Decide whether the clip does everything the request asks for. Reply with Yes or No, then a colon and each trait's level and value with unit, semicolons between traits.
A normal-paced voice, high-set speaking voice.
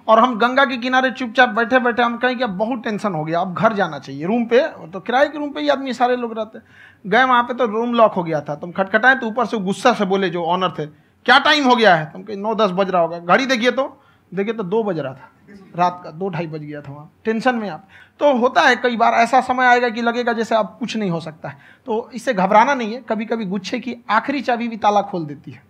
No: fast, 270 wpm; high, 225 Hz